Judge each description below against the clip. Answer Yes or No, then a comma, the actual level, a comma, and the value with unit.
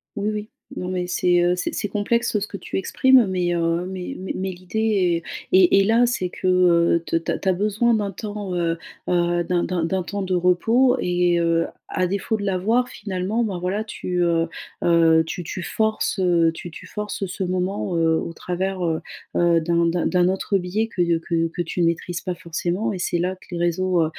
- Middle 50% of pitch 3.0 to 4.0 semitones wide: No, narrow, 2.5 semitones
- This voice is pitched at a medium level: Yes, medium, 180 Hz